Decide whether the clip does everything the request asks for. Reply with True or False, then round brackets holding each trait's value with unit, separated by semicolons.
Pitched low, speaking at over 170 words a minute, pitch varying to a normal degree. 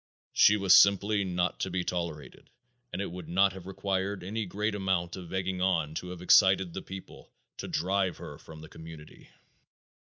False (95 Hz; 180 wpm; 2.0 semitones)